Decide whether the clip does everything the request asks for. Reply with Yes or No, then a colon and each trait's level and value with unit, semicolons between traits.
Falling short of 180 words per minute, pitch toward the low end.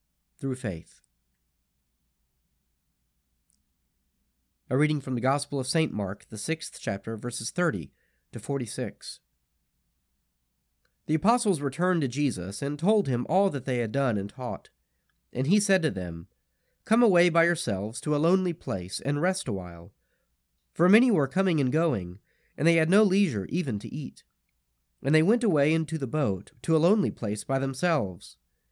Yes: average, 160 wpm; low, 130 Hz